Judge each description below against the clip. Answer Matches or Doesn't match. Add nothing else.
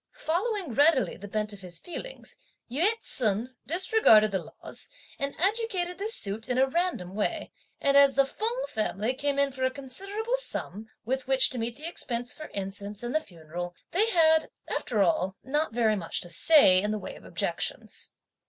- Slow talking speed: Doesn't match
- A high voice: Matches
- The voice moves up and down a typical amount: Doesn't match